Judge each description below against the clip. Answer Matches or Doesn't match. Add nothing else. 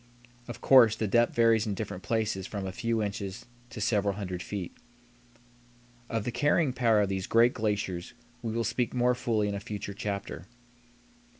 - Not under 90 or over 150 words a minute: Doesn't match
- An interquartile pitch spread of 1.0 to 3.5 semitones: Matches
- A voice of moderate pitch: Doesn't match